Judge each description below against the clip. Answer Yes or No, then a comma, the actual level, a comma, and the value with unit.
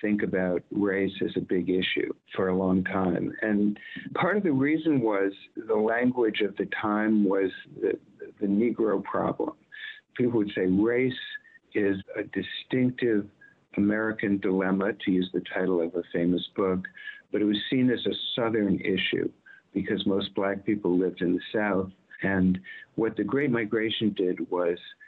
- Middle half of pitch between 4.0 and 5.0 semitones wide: Yes, average, 4.6 semitones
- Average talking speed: Yes, average, 160 wpm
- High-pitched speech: No, low, 105 Hz